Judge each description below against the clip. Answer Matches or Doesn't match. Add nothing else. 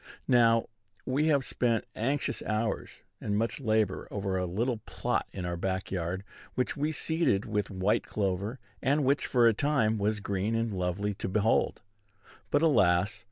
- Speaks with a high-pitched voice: Doesn't match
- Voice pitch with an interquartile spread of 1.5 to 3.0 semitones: Doesn't match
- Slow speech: Doesn't match